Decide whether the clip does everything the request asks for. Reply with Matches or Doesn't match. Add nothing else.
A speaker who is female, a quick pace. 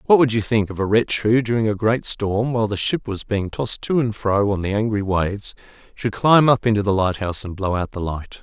Doesn't match